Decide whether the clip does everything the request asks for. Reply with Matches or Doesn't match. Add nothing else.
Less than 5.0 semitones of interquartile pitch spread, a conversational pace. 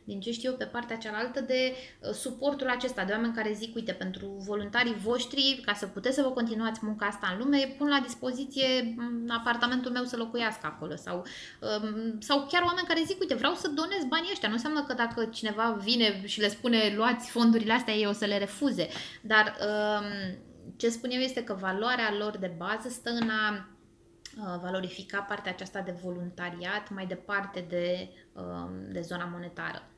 Doesn't match